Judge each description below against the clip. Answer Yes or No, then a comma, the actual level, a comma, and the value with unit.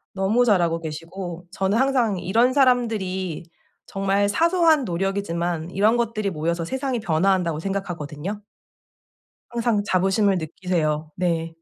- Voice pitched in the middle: No, high, 195 Hz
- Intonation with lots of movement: No, average, 4.6 semitones